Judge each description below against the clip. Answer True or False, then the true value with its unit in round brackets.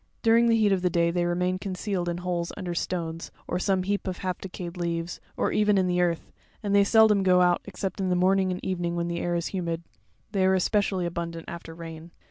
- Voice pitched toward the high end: False (180 Hz)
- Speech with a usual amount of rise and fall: False (2.0 semitones)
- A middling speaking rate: False (235 wpm)